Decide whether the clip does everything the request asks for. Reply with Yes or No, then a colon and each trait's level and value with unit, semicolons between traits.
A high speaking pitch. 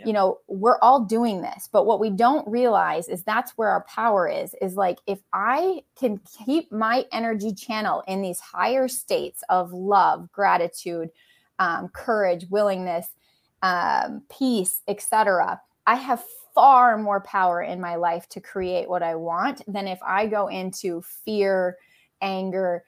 Yes: high, 200 Hz